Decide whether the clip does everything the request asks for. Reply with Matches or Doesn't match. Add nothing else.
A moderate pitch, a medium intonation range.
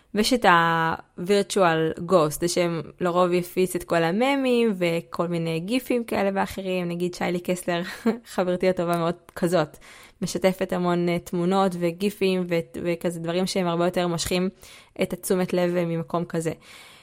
Doesn't match